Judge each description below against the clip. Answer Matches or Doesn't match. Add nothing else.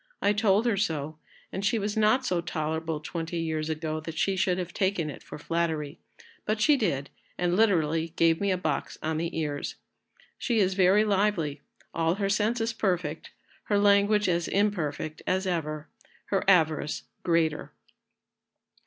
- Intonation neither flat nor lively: Matches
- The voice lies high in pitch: Doesn't match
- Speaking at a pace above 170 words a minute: Doesn't match